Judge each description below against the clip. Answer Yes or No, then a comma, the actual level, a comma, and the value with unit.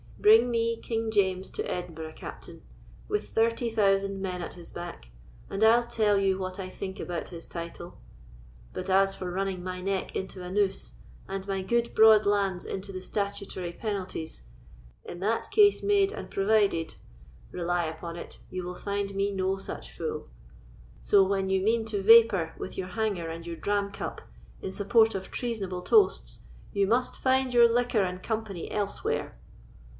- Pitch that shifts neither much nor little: Yes, average, 3.2 semitones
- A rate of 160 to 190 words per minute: Yes, average, 170 wpm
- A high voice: Yes, high, 195 Hz